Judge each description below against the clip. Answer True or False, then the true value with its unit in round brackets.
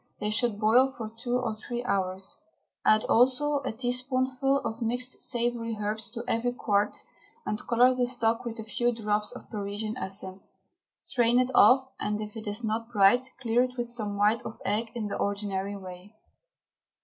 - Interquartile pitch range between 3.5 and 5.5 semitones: False (2.9 semitones)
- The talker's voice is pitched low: False (230 Hz)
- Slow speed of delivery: False (175 wpm)